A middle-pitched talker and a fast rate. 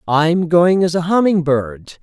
Yes: medium, 165 Hz; fast, 210 wpm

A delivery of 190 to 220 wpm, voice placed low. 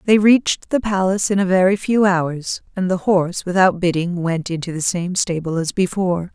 No: average, 200 wpm; medium, 185 Hz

